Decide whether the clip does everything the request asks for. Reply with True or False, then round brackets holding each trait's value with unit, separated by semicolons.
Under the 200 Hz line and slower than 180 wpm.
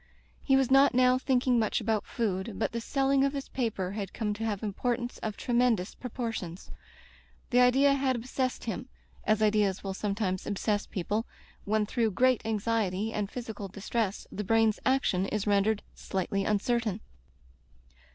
False (220 Hz; 160 wpm)